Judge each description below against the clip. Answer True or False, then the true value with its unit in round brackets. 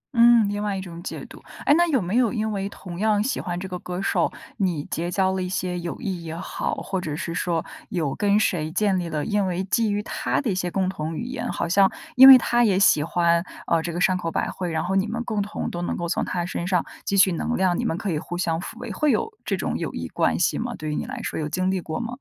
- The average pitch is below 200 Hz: True (185 Hz)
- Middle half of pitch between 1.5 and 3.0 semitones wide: False (3.5 semitones)